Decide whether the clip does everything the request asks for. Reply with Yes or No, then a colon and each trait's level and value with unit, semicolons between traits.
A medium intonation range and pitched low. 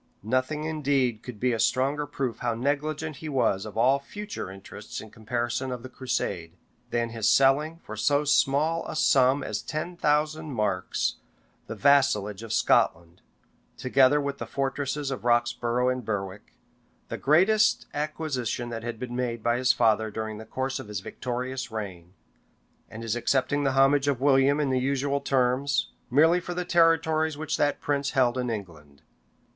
Yes: average, 3.9 semitones; low, 130 Hz